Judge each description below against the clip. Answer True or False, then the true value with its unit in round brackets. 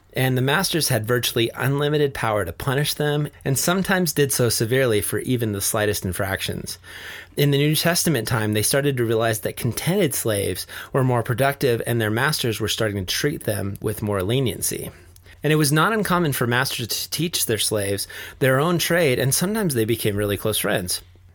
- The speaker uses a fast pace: False (190 wpm)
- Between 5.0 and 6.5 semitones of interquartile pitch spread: True (5.5 semitones)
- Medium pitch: False (125 Hz)